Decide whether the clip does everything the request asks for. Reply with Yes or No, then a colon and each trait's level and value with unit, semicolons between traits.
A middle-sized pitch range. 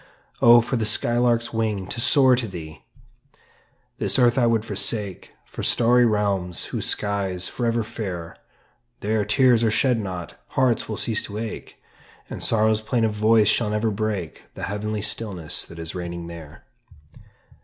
Yes: average, 3.1 semitones